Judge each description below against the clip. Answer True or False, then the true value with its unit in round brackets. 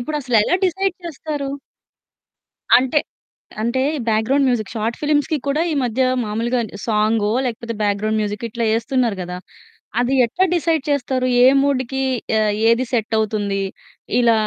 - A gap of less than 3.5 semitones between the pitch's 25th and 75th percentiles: False (4.2 semitones)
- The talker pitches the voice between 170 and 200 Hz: False (240 Hz)